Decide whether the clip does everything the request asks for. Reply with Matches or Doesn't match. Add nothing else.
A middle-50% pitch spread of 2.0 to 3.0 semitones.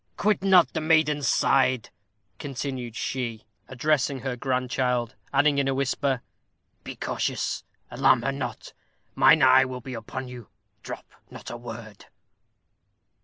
Matches